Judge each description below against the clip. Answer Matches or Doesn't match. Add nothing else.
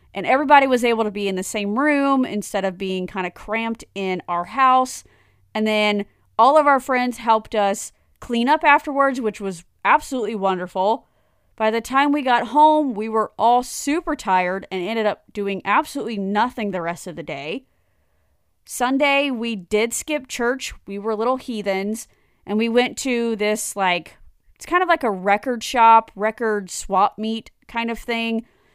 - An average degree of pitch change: Matches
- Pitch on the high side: Matches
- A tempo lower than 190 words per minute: Matches